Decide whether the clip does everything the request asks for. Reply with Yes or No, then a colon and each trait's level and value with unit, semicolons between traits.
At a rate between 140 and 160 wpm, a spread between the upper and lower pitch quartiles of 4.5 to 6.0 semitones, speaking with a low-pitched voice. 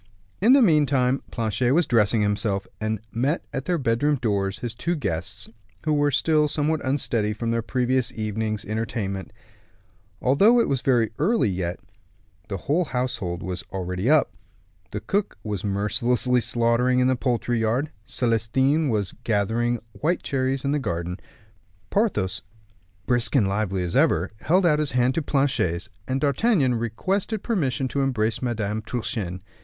Yes: average, 150 wpm; average, 5.0 semitones; low, 120 Hz